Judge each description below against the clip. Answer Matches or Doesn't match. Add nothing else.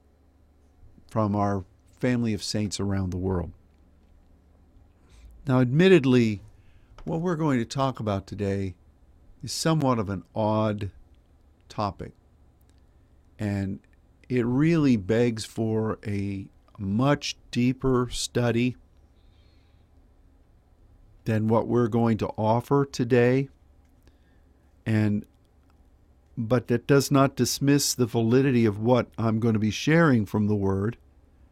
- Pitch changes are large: Matches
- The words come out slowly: Matches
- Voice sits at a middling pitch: Doesn't match